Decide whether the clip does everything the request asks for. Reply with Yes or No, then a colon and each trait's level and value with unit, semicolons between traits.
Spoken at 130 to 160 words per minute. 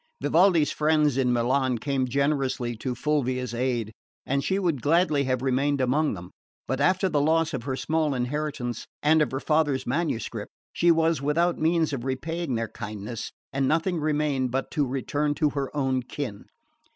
No: average, 170 wpm